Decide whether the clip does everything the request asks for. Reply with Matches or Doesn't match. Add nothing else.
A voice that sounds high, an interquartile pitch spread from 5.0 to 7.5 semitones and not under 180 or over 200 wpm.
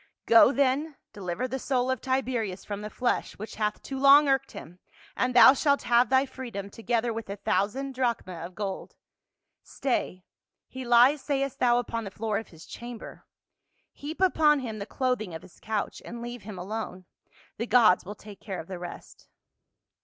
Doesn't match